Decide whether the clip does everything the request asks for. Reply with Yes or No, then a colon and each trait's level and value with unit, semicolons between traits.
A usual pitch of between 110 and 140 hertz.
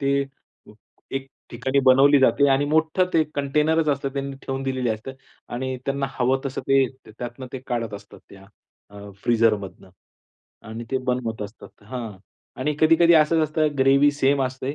Yes: low, 135 Hz